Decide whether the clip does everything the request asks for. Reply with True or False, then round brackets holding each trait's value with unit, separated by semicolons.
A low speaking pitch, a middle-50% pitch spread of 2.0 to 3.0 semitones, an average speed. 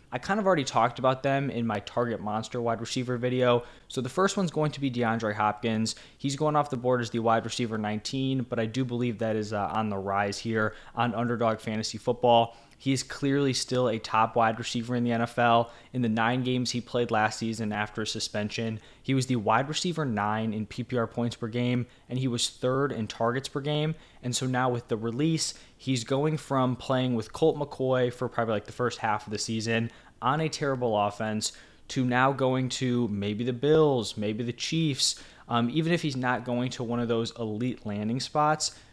False (120 Hz; 2.7 semitones; 215 wpm)